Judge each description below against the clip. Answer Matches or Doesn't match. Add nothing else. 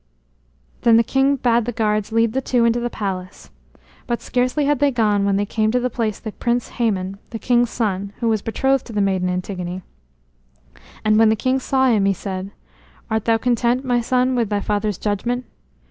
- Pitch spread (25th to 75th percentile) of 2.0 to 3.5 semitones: Matches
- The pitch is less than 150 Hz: Doesn't match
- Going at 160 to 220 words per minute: Matches